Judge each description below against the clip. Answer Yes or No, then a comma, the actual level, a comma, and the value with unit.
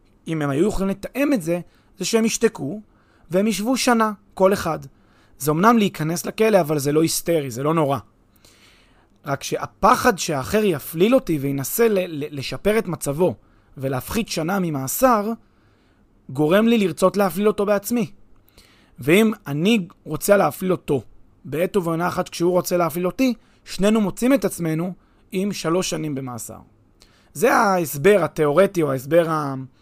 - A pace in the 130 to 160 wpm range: Yes, average, 140 wpm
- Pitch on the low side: No, medium, 175 Hz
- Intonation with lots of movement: Yes, wide, 6.2 semitones